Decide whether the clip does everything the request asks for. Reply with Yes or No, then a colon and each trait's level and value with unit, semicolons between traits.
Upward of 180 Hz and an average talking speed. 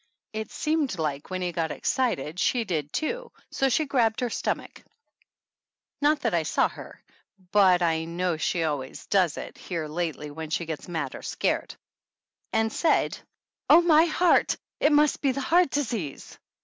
Yes: high, 190 Hz; average, 165 wpm